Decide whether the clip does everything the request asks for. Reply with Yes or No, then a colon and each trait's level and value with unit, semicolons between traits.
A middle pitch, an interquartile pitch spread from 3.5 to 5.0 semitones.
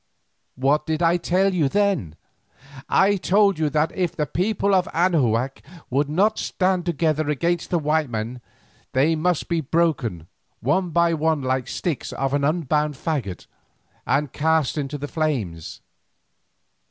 Yes: medium, 155 Hz; average, 4.1 semitones